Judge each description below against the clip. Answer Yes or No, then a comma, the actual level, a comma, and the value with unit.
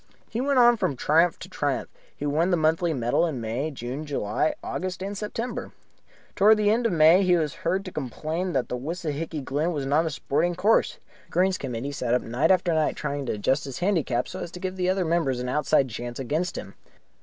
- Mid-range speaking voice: Yes, medium, 160 Hz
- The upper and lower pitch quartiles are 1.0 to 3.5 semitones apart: No, average, 5.2 semitones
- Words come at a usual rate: No, fast, 215 wpm